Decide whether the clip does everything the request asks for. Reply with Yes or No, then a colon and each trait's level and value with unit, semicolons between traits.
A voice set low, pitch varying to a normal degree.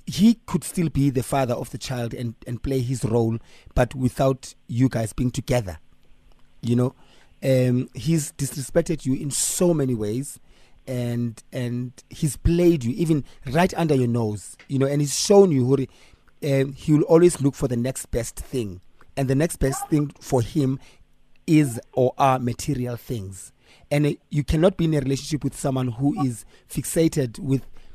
Yes: low, 130 Hz; average, 3.4 semitones